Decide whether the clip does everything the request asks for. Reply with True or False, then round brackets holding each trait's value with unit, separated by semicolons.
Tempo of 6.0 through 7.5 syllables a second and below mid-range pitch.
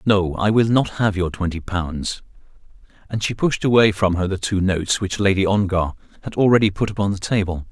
False (5.4 syllables/s; 100 Hz)